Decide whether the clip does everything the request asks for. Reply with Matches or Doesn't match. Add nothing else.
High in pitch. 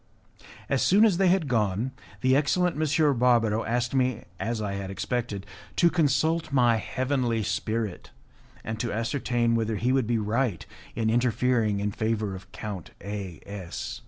Doesn't match